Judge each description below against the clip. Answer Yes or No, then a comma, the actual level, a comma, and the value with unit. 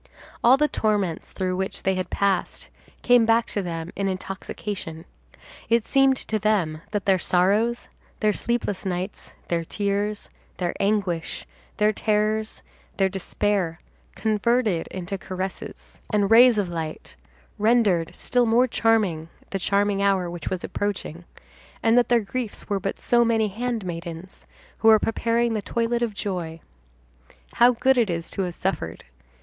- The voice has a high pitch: Yes, high, 205 Hz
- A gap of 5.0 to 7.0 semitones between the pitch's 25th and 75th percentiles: No, average, 3.7 semitones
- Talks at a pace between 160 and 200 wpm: No, average, 145 wpm